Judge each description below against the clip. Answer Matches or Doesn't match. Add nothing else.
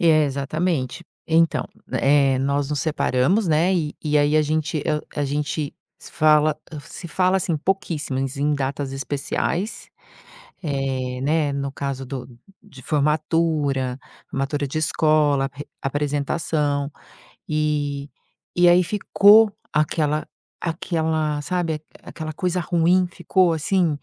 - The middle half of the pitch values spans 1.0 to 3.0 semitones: Matches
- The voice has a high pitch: Doesn't match